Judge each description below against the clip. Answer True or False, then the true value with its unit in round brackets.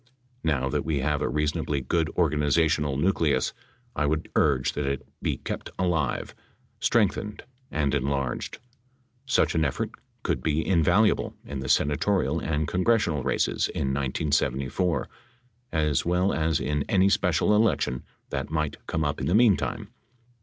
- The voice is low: True (75 Hz)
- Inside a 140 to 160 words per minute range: True (145 wpm)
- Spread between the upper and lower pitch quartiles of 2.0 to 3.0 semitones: False (3.5 semitones)